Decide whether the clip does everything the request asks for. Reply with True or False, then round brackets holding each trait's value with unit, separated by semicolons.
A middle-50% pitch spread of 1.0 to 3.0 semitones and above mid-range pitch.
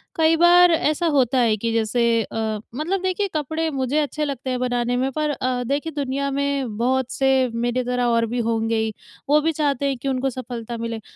False (3.7 semitones; 260 Hz)